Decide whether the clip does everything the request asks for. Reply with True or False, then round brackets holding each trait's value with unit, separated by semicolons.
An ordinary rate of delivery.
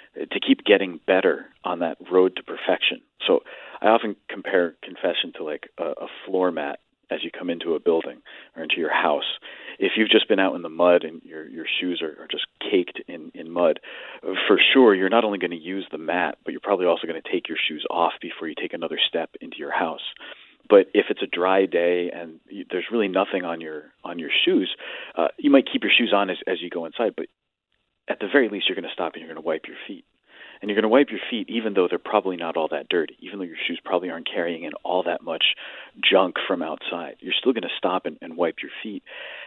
False (245 wpm)